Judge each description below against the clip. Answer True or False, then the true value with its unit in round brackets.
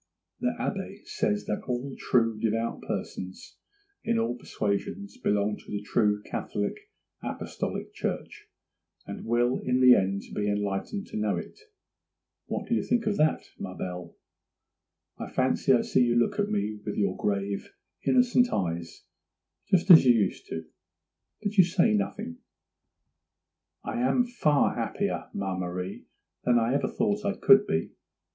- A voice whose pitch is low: True (120 Hz)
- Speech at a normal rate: True (150 wpm)